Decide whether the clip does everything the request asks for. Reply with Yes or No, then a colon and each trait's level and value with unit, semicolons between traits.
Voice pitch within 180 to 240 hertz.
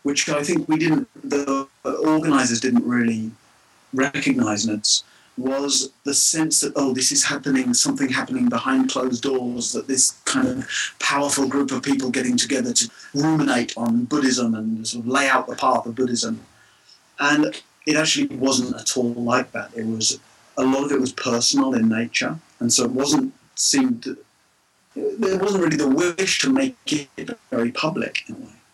No: medium, 140 Hz